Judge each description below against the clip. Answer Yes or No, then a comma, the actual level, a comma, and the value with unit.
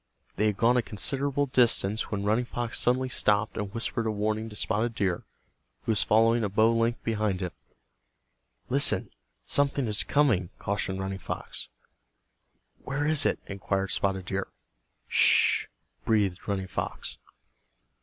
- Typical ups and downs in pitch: Yes, average, 3.2 semitones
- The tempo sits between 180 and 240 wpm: No, average, 145 wpm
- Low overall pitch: Yes, low, 110 Hz